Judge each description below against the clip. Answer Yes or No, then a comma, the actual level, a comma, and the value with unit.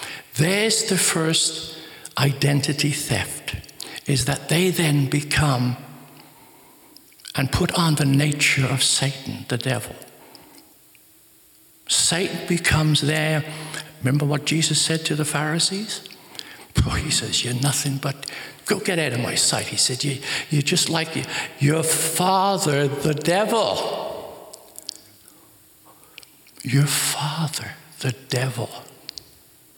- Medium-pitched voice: Yes, medium, 150 Hz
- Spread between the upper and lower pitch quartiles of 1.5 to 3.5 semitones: Yes, average, 2.7 semitones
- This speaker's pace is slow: Yes, slow, 110 wpm